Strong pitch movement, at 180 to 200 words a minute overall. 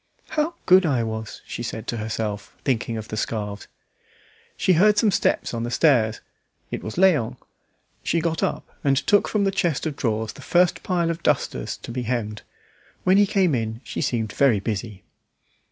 Yes: wide, 7.8 semitones; average, 185 wpm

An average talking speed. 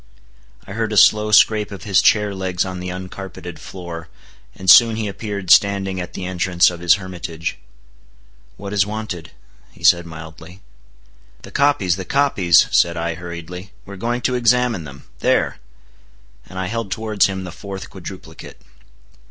Yes: average, 160 wpm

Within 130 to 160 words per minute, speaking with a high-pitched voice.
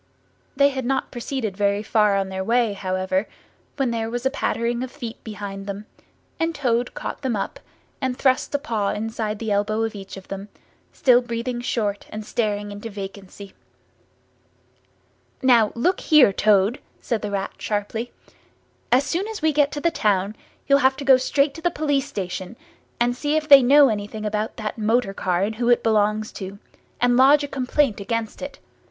No: average, 185 wpm; high, 230 Hz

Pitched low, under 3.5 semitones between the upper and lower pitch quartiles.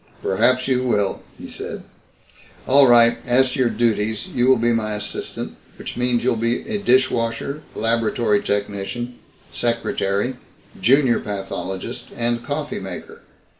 Yes: low, 120 Hz; average, 3.1 semitones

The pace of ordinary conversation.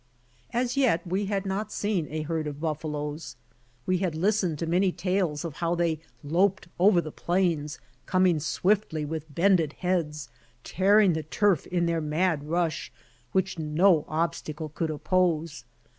Yes: average, 150 wpm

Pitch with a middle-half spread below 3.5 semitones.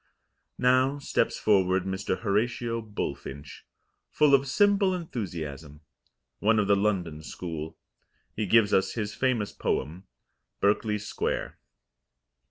No: average, 4.9 semitones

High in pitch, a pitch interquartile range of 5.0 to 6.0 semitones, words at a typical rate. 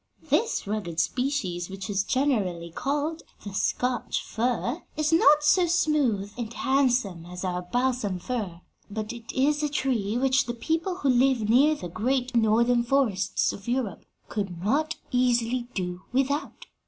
Yes: high, 245 Hz; wide, 5.4 semitones; average, 150 wpm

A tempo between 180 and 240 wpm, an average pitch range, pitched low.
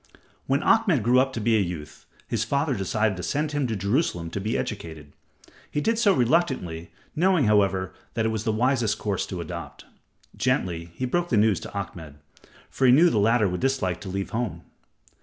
No: average, 195 wpm; wide, 6.1 semitones; low, 110 Hz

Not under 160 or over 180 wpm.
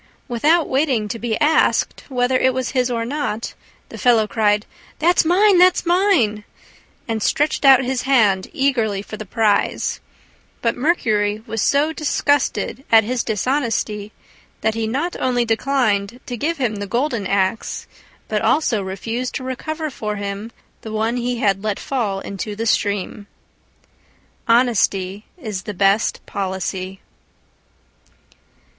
No: average, 140 wpm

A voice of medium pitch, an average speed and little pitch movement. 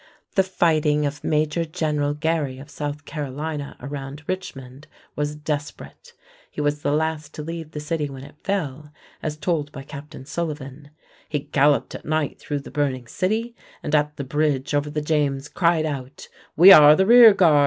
Yes: medium, 150 Hz; average, 175 wpm; narrow, 1.7 semitones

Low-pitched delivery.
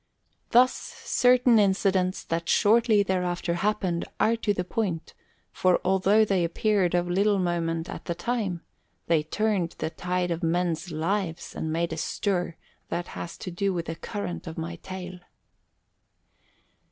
No: medium, 180 Hz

